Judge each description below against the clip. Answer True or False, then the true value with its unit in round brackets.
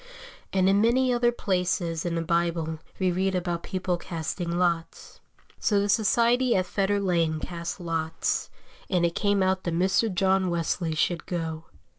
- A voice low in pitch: False (180 Hz)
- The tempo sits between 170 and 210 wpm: False (160 wpm)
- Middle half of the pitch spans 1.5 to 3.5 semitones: True (2.6 semitones)